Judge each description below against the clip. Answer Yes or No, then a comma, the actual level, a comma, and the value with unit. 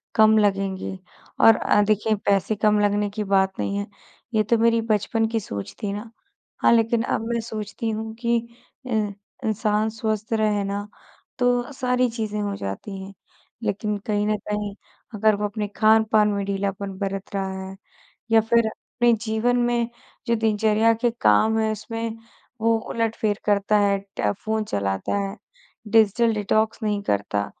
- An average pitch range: No, narrow, 1.9 semitones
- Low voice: No, high, 215 Hz